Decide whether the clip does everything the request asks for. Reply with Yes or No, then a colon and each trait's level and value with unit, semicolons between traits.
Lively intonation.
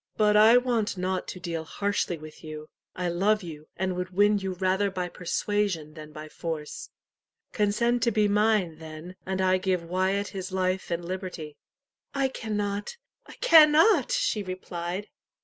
No: average, 3.3 semitones